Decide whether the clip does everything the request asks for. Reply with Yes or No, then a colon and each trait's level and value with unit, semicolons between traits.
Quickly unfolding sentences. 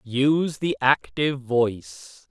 No: slow, 105 wpm